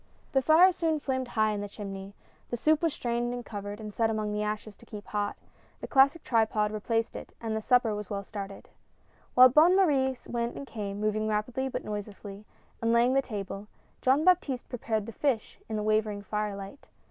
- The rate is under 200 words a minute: No, fast, 205 wpm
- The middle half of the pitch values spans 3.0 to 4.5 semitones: Yes, average, 3.8 semitones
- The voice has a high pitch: Yes, high, 220 Hz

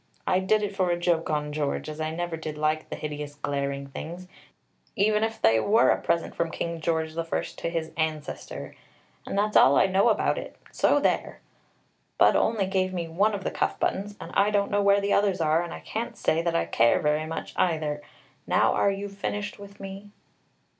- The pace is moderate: No, fast, 210 wpm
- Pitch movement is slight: No, average, 4.3 semitones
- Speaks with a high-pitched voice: No, medium, 170 Hz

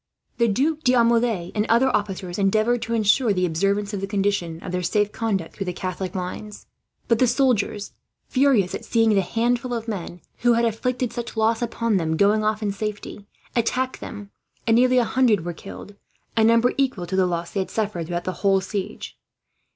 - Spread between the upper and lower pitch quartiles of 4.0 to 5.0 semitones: No, average, 3.5 semitones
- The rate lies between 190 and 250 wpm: Yes, average, 195 wpm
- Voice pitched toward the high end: Yes, high, 210 Hz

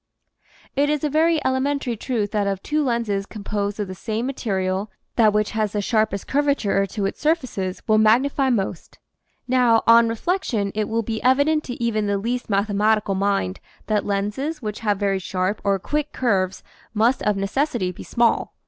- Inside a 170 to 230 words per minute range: Yes, average, 175 wpm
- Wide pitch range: No, average, 4.3 semitones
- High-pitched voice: Yes, high, 215 Hz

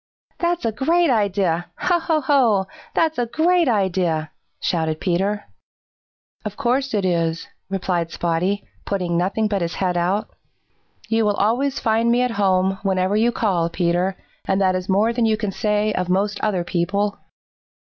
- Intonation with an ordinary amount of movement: Yes, average, 3.9 semitones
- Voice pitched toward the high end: Yes, high, 200 Hz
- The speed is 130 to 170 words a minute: Yes, average, 160 wpm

